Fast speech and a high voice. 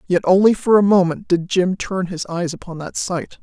No: fast, 230 wpm; medium, 180 Hz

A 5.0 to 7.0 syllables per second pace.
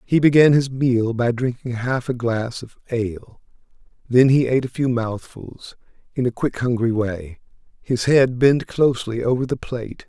No: 4.7 syllables/s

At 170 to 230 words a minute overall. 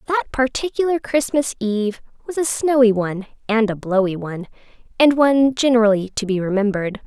No: average, 155 wpm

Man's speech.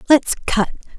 No: female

